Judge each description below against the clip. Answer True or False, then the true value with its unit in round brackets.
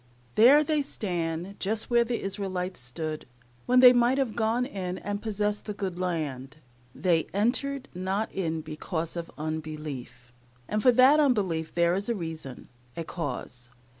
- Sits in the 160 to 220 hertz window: True (185 Hz)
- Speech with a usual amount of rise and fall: False (6.0 semitones)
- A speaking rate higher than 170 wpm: False (155 wpm)